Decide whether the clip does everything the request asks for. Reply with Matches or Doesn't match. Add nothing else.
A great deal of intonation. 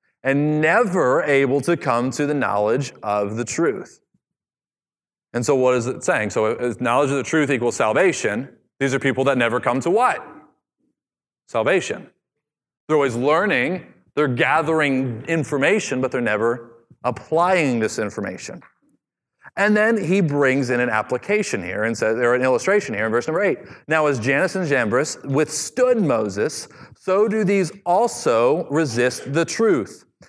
Matches